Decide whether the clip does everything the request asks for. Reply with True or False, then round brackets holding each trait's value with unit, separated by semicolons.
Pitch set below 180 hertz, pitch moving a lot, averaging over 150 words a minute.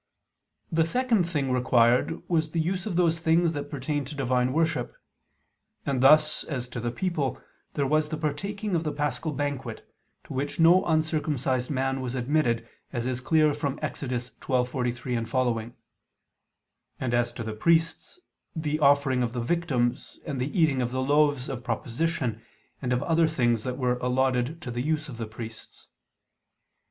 False (140 Hz; 4.1 semitones; 165 wpm)